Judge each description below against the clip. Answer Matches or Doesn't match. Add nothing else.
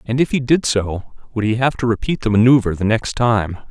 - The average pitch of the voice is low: Matches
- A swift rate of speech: Matches